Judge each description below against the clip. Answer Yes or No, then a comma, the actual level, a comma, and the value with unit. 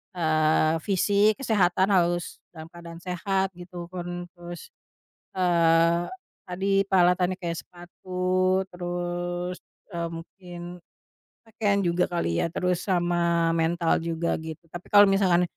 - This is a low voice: No, medium, 175 Hz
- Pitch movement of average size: No, narrow, 1.5 semitones